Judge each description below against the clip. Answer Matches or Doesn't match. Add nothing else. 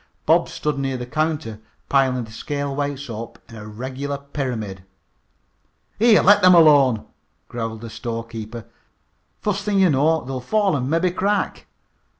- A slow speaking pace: Doesn't match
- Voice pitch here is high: Doesn't match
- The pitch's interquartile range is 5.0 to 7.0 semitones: Matches